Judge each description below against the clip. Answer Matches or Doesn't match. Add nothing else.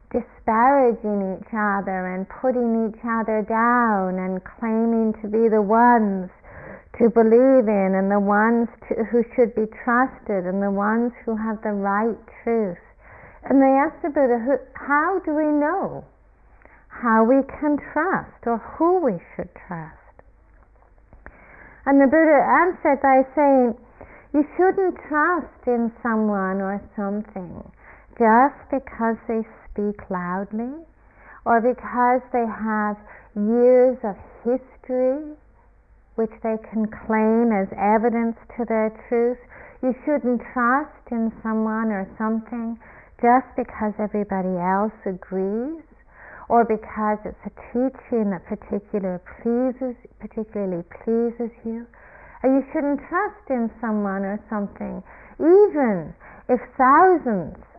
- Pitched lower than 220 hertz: Doesn't match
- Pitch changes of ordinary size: Matches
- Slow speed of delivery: Matches